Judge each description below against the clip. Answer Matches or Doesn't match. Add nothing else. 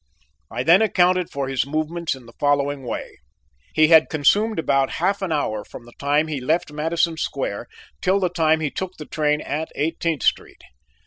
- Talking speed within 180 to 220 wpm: Matches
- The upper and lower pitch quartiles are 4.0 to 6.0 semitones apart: Doesn't match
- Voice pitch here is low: Doesn't match